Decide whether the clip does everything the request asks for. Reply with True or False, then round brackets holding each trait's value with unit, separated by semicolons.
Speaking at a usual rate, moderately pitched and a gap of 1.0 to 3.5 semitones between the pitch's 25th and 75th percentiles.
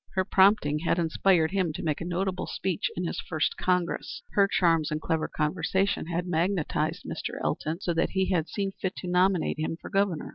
True (195 wpm; 175 Hz; 2.8 semitones)